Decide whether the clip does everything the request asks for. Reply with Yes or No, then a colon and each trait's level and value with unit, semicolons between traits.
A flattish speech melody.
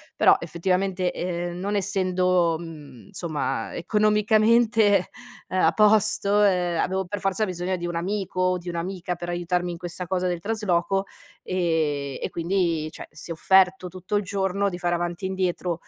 Yes: narrow, 2.2 semitones